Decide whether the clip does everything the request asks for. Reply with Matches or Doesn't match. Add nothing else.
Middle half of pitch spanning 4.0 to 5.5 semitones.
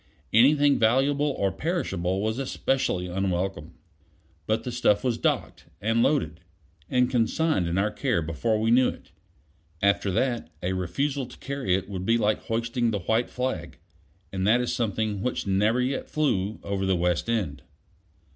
Matches